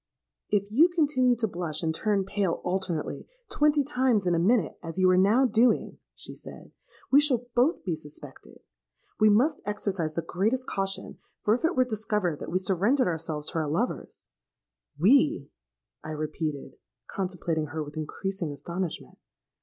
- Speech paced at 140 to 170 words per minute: Yes, average, 155 wpm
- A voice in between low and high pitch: No, high, 195 Hz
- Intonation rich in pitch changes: Yes, wide, 6.8 semitones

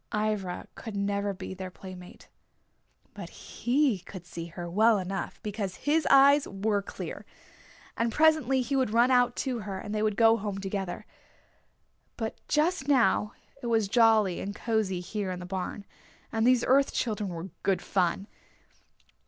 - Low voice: No, high, 210 Hz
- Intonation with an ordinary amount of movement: Yes, average, 3.9 semitones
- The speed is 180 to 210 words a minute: No, average, 160 wpm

